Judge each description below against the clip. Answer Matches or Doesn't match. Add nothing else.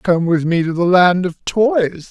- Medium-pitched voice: Matches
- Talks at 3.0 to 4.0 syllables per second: Matches